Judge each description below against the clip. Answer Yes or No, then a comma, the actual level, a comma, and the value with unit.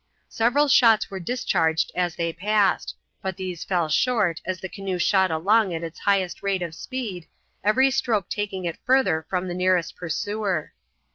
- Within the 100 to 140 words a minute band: No, average, 165 wpm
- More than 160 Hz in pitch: Yes, high, 190 Hz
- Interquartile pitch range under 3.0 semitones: No, average, 3.7 semitones